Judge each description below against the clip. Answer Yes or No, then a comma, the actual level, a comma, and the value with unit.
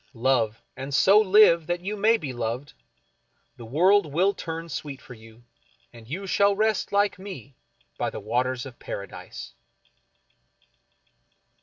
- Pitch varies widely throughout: Yes, wide, 8.2 semitones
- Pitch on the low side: No, medium, 150 Hz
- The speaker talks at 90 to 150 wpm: Yes, average, 145 wpm